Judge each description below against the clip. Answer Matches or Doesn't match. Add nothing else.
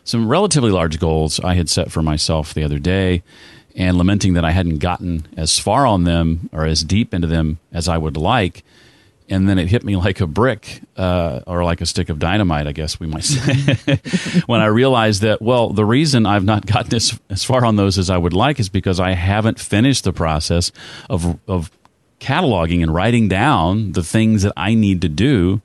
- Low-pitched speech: Matches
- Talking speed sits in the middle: Doesn't match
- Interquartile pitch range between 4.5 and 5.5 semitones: Matches